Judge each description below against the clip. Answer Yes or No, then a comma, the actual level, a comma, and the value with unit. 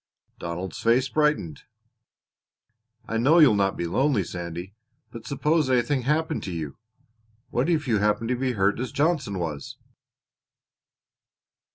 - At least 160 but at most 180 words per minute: No, average, 145 wpm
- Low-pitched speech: Yes, low, 115 Hz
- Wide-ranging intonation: Yes, wide, 7.1 semitones